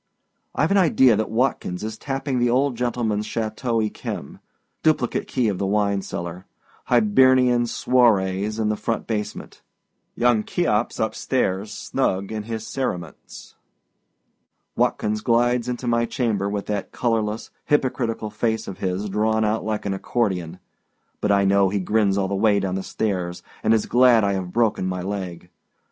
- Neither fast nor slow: Yes, average, 155 wpm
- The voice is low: Yes, low, 110 Hz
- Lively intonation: No, average, 3.3 semitones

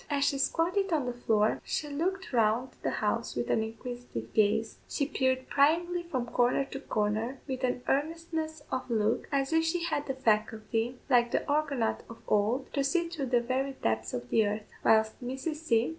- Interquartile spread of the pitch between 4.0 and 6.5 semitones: Yes, average, 4.9 semitones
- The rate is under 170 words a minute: No, average, 190 wpm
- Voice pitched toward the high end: Yes, very high, 260 Hz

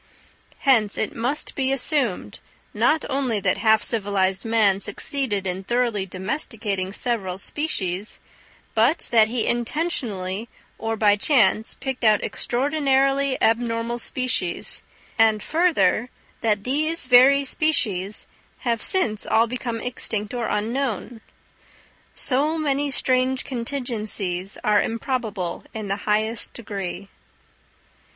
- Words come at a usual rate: No, slow, 110 wpm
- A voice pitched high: Yes, high, 230 Hz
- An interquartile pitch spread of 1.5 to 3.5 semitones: No, average, 4.4 semitones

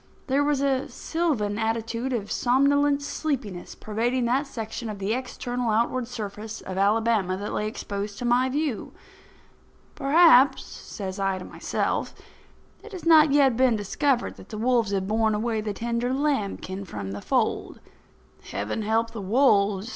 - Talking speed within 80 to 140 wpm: No, average, 155 wpm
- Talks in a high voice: Yes, high, 230 Hz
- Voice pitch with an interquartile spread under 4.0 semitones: No, average, 4.3 semitones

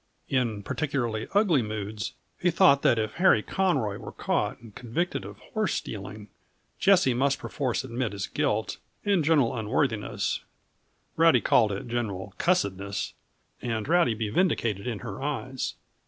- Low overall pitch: Yes, low, 120 Hz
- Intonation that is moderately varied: No, wide, 5.8 semitones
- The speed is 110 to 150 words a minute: Yes, average, 140 wpm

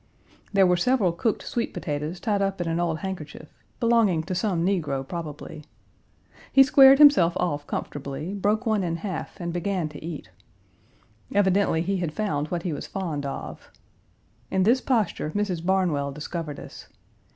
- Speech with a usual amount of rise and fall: Yes, average, 4.2 semitones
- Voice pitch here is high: No, medium, 180 Hz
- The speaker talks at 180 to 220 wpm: No, average, 160 wpm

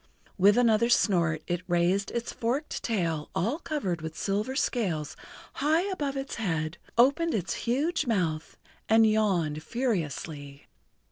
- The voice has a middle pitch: No, high, 205 Hz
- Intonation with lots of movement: Yes, wide, 6.8 semitones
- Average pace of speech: No, slow, 130 wpm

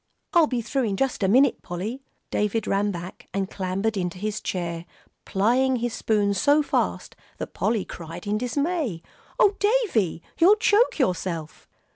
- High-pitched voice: Yes, high, 215 Hz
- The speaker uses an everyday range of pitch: No, wide, 6.2 semitones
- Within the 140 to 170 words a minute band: Yes, average, 155 wpm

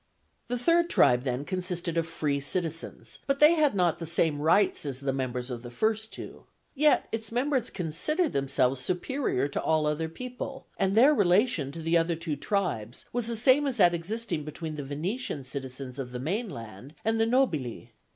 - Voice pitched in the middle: Yes, medium, 170 Hz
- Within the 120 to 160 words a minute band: No, average, 185 wpm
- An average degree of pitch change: No, wide, 8.5 semitones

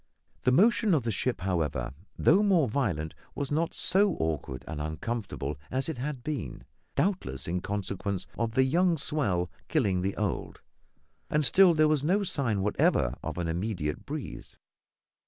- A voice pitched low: Yes, low, 115 Hz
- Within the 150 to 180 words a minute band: Yes, average, 155 wpm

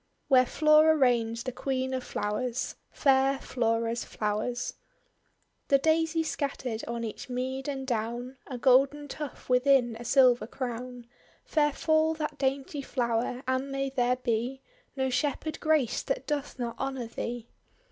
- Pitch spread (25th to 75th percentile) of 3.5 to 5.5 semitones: No, narrow, 2.5 semitones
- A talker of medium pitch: No, very high, 260 Hz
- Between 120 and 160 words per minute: Yes, average, 140 wpm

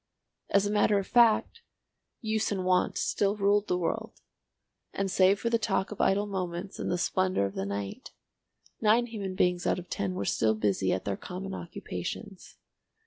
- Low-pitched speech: No, high, 190 Hz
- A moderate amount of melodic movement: Yes, average, 3.2 semitones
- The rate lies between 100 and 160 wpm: No, average, 180 wpm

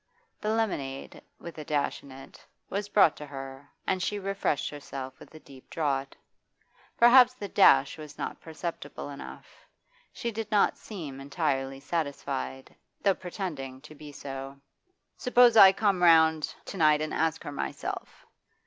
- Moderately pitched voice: Yes, medium, 155 Hz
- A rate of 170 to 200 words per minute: No, average, 150 wpm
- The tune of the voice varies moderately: No, wide, 6.1 semitones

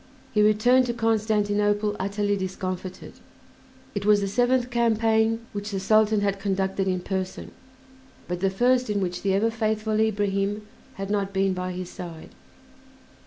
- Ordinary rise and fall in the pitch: No, narrow, 2.2 semitones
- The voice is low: No, high, 205 Hz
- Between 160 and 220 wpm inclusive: No, average, 150 wpm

